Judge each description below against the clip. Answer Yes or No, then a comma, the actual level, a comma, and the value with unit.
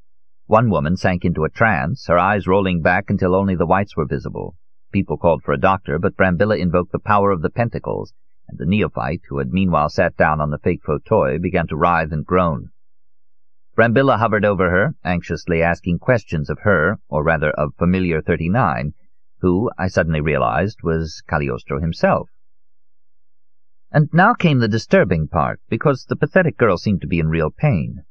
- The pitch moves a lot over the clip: No, average, 3.2 semitones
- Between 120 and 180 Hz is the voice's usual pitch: No, very low, 90 Hz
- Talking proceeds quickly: No, average, 180 wpm